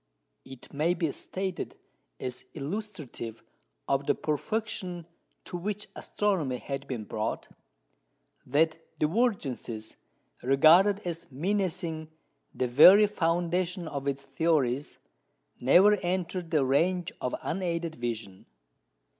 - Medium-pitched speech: Yes, medium, 160 Hz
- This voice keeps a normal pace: No, slow, 105 wpm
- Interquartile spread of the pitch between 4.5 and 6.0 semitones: Yes, average, 5.2 semitones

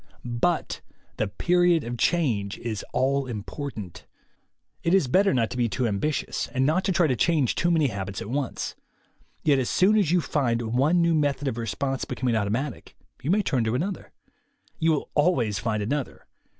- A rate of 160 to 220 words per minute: Yes, average, 180 wpm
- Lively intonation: Yes, wide, 5.9 semitones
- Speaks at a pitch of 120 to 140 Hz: Yes, low, 135 Hz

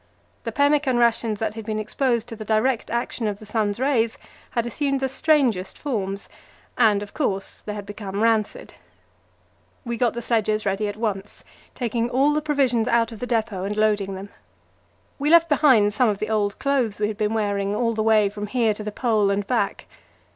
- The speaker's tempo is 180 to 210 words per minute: Yes, average, 195 wpm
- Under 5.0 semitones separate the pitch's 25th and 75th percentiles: Yes, average, 3.0 semitones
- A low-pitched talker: No, high, 220 Hz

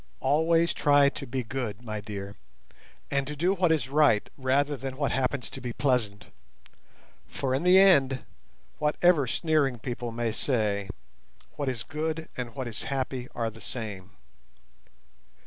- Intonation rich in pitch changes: No, average, 4.1 semitones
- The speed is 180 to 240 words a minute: No, average, 150 wpm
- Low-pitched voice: Yes, low, 130 Hz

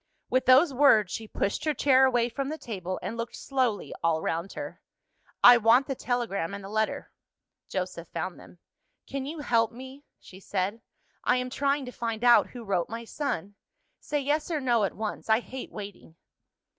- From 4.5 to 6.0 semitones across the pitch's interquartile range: Yes, average, 4.8 semitones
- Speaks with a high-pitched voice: Yes, high, 235 Hz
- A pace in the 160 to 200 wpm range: Yes, average, 185 wpm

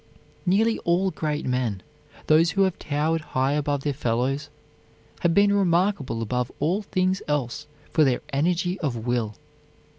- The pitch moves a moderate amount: No, wide, 5.8 semitones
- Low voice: No, medium, 150 Hz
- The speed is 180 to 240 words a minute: No, average, 145 wpm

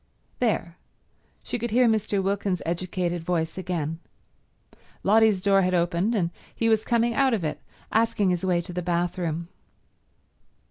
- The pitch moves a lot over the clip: No, average, 4.2 semitones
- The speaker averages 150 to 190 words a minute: No, average, 140 wpm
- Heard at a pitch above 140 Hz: Yes, medium, 185 Hz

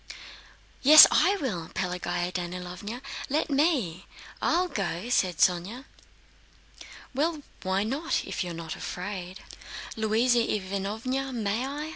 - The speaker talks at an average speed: No, slow, 110 wpm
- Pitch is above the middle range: Yes, high, 210 Hz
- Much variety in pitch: Yes, wide, 6.9 semitones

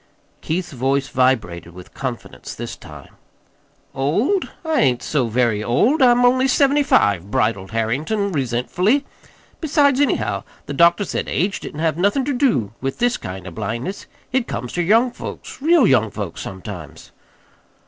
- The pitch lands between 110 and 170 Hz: Yes, medium, 140 Hz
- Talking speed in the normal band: Yes, average, 150 wpm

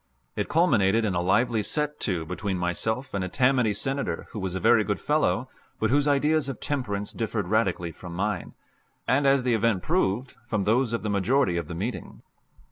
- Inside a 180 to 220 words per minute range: Yes, average, 195 wpm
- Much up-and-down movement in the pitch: Yes, wide, 5.9 semitones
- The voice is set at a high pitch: No, low, 110 Hz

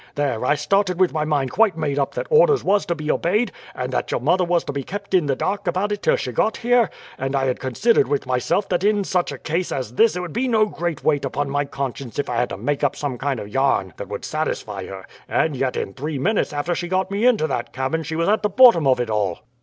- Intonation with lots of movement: Yes, wide, 6.4 semitones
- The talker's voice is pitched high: No, medium, 155 Hz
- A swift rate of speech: Yes, fast, 270 wpm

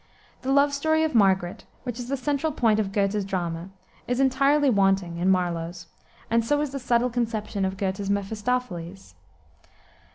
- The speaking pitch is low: No, high, 215 Hz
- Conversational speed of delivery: Yes, average, 160 wpm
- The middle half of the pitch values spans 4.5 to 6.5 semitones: Yes, wide, 5.5 semitones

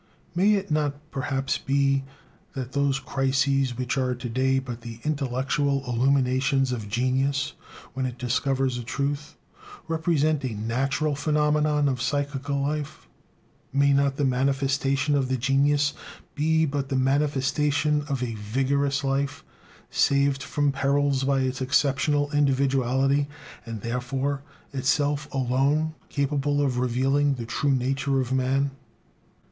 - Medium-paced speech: No, slow, 130 wpm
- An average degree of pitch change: No, narrow, 1.6 semitones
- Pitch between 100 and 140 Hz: Yes, low, 135 Hz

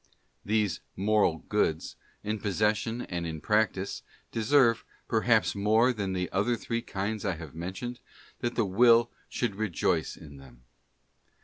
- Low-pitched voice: Yes, low, 105 Hz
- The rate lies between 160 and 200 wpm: No, slow, 135 wpm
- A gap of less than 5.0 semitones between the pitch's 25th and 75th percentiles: Yes, average, 3.8 semitones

